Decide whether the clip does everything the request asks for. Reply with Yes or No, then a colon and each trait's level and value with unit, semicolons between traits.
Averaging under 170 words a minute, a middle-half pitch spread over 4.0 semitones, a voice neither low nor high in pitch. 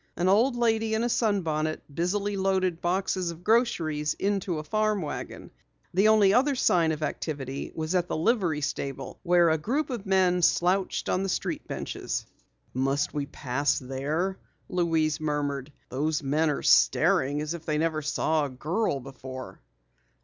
Yes: average, 160 wpm; average, 4.6 semitones; medium, 165 Hz